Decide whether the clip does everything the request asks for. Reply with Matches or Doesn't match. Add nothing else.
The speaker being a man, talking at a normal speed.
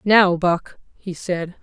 Doesn't match